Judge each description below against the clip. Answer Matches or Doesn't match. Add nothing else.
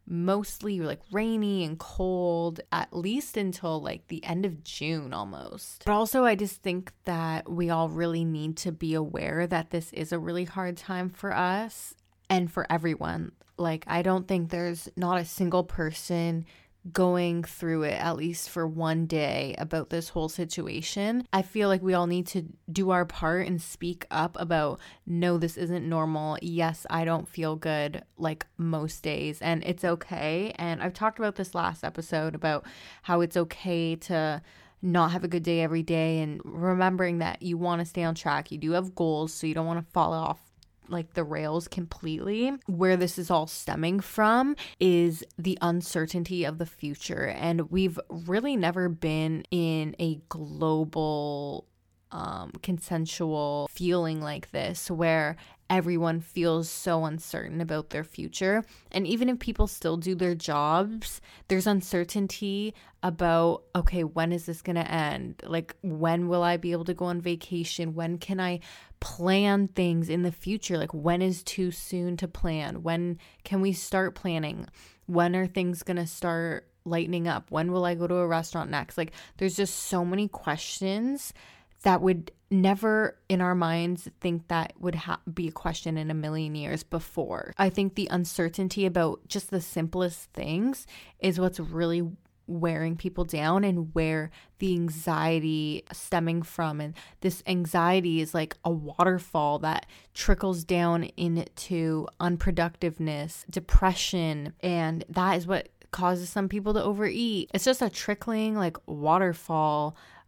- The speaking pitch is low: Doesn't match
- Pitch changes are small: Matches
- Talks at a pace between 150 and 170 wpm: Matches